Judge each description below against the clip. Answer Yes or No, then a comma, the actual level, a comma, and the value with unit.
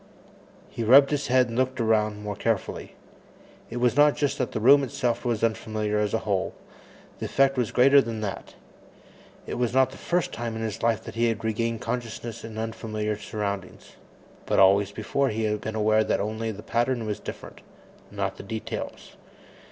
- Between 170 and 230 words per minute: Yes, average, 185 wpm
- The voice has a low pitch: Yes, low, 115 Hz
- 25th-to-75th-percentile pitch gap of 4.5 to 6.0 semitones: No, narrow, 2.4 semitones